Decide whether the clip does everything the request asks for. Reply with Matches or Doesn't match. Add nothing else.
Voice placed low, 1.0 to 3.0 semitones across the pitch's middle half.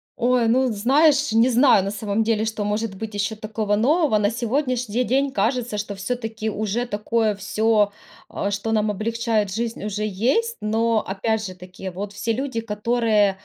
Doesn't match